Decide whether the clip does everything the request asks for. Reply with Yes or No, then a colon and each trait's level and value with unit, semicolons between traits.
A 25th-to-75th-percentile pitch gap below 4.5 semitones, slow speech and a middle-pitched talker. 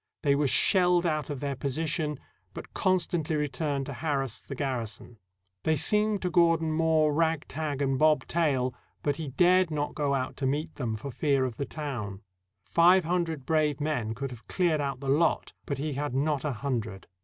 No: average, 3.2 semitones; average, 190 wpm; medium, 145 Hz